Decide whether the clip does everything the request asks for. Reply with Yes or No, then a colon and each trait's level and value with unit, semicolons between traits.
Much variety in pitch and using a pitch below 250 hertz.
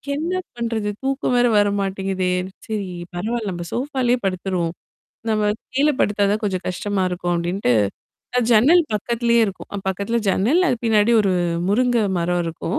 No: average, 4.1 semitones; high, 210 Hz